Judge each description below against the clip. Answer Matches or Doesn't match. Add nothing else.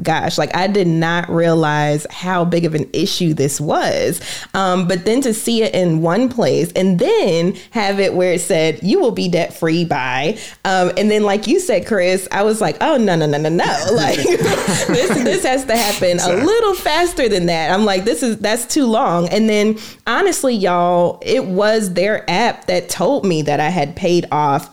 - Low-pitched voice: Doesn't match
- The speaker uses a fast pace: Matches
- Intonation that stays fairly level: Doesn't match